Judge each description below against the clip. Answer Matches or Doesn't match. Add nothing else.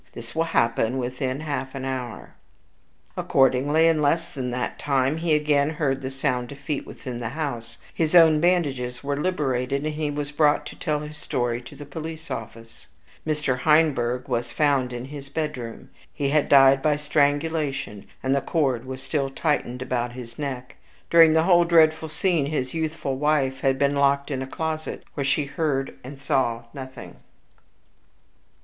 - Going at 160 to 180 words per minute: Matches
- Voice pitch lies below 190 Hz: Matches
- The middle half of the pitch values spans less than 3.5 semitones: Matches